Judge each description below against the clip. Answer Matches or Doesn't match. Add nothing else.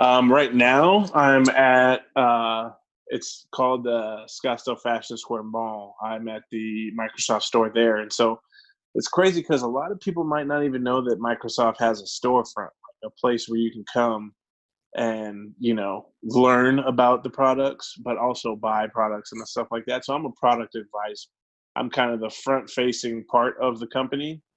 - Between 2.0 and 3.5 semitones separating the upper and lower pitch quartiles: Matches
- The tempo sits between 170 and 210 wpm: Matches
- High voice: Doesn't match